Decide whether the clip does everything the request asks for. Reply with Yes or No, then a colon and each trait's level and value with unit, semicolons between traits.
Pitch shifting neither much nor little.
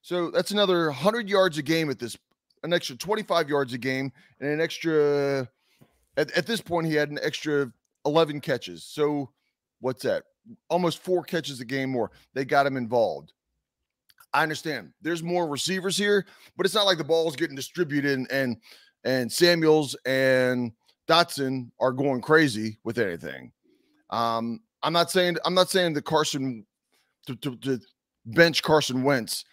Yes: average, 4.8 semitones